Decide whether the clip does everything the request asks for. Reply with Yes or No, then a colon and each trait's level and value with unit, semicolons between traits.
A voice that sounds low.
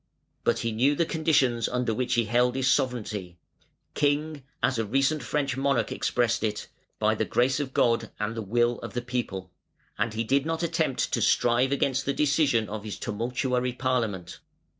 Yes: low, 125 Hz